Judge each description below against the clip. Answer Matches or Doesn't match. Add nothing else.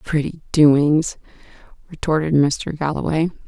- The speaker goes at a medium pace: Doesn't match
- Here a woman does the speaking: Matches